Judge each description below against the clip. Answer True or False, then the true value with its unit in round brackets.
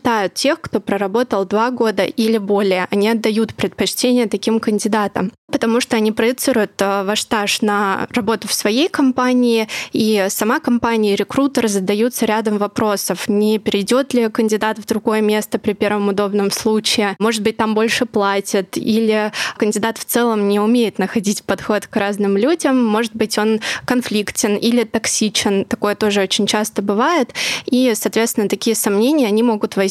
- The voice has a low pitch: False (220 Hz)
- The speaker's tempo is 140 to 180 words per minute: True (155 wpm)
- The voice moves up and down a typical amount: False (2.2 semitones)